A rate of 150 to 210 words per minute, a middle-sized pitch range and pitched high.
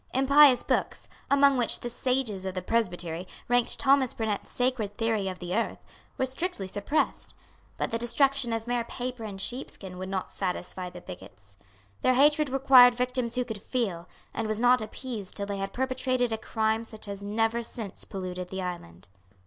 Yes: average, 180 wpm; average, 4.7 semitones; high, 225 Hz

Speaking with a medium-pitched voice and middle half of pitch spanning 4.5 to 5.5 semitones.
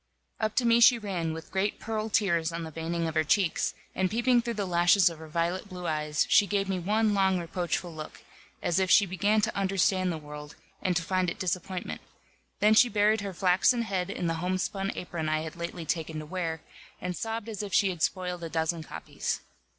No: medium, 180 Hz; average, 3.5 semitones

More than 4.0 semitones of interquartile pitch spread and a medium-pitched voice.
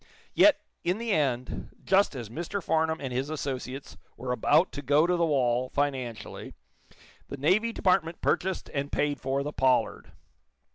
Yes: average, 4.6 semitones; medium, 145 Hz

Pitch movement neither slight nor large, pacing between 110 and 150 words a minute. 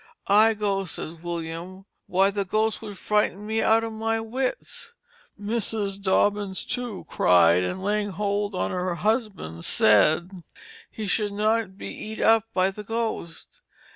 Yes: average, 3.0 semitones; average, 145 wpm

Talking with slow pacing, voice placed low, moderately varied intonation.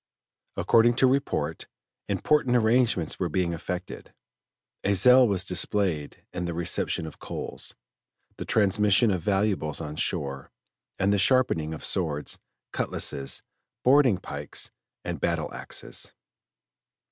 No: slow, 120 wpm; very low, 95 Hz; wide, 5.9 semitones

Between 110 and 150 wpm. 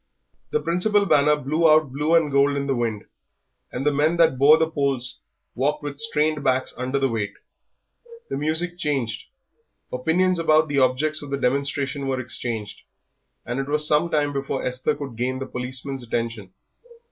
No: average, 170 wpm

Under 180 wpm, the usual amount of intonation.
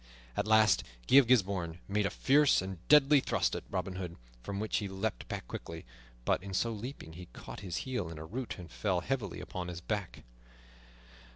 No: average, 195 wpm; average, 4.7 semitones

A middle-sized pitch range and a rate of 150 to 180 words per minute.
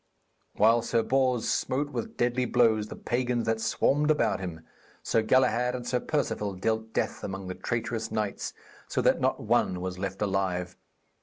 Yes: average, 3.9 semitones; average, 165 wpm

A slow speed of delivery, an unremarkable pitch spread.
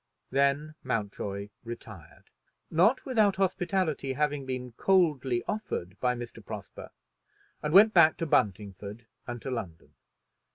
No: slow, 120 wpm; wide, 7.1 semitones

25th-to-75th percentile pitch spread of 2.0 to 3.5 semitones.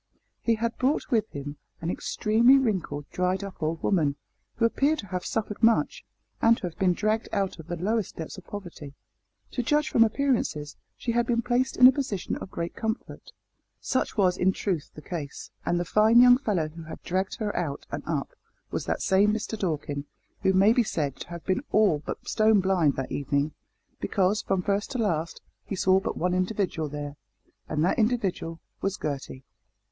No: average, 5.3 semitones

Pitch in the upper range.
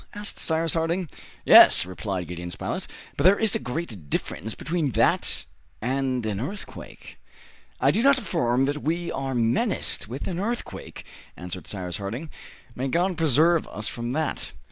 No: low, 135 Hz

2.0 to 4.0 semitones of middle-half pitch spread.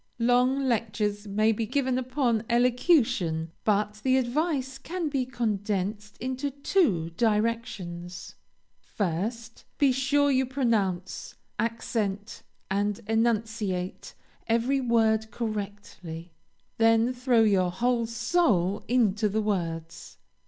Yes: average, 3.7 semitones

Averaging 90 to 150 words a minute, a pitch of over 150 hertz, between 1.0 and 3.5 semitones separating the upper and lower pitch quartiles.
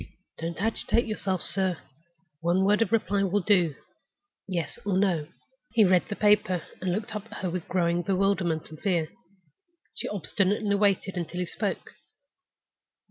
Yes: average, 145 wpm; high, 190 Hz; average, 2.8 semitones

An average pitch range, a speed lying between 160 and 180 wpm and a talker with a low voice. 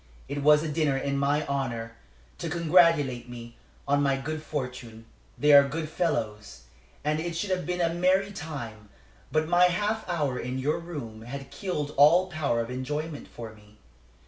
No: average, 4.8 semitones; average, 170 wpm; medium, 145 Hz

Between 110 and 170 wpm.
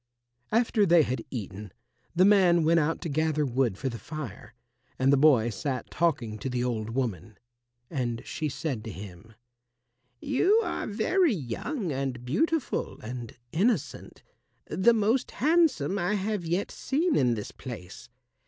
Yes: average, 150 wpm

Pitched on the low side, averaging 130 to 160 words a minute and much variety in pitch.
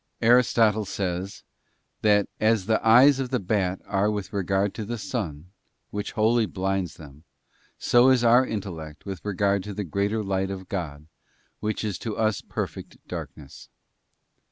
No: low, 100 Hz; average, 155 wpm; average, 2.8 semitones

